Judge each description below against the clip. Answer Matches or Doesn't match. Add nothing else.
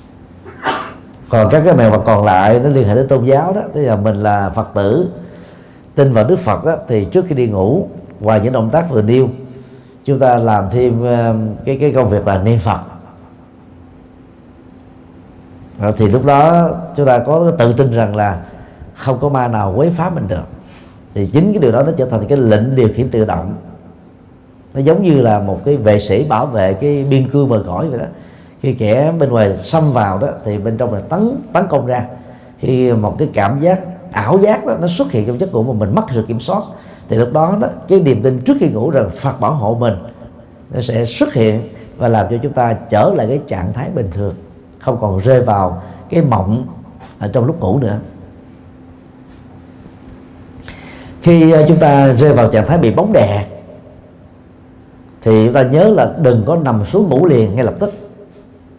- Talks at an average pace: Matches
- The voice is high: Doesn't match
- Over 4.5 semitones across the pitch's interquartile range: Matches